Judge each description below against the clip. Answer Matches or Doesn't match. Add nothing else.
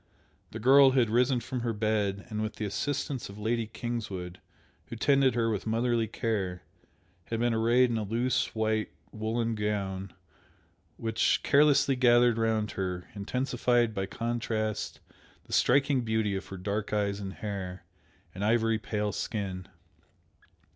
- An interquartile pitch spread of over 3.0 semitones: Doesn't match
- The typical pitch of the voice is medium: Doesn't match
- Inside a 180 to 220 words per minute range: Doesn't match